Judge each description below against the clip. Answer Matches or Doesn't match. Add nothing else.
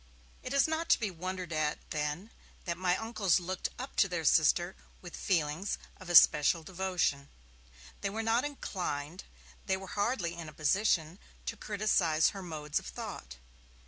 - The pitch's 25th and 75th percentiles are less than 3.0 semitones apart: Doesn't match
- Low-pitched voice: Doesn't match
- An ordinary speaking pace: Matches